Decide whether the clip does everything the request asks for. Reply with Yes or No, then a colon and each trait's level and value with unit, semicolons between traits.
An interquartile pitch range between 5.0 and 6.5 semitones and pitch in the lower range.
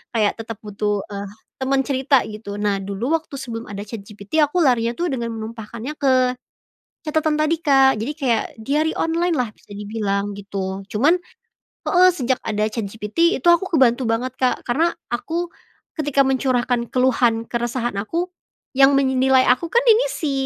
No: average, 5.3 semitones; very high, 250 Hz